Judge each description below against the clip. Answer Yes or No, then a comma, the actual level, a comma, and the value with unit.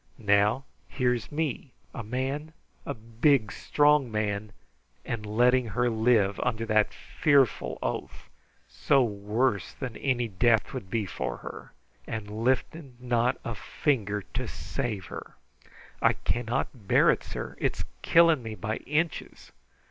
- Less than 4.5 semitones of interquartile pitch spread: Yes, average, 3.7 semitones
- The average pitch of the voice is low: Yes, low, 115 Hz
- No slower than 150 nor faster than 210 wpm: No, slow, 135 wpm